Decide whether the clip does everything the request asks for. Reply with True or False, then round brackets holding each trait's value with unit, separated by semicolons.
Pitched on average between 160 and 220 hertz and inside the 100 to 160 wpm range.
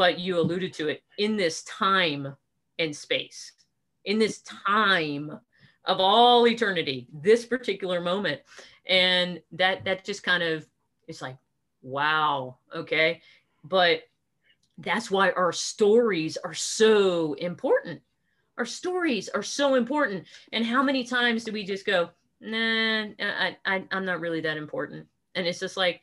True (185 Hz; 145 wpm)